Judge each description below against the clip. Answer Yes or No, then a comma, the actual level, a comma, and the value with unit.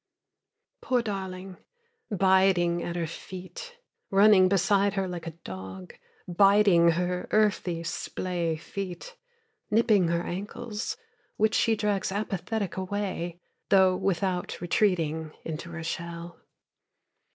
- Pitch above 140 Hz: Yes, medium, 185 Hz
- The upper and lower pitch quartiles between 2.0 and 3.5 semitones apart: Yes, average, 2.9 semitones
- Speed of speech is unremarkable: No, slow, 105 wpm